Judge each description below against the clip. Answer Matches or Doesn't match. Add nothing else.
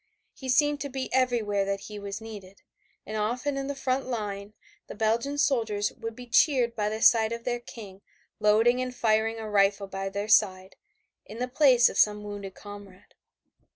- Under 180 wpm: Doesn't match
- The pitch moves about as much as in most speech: Matches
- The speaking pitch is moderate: Doesn't match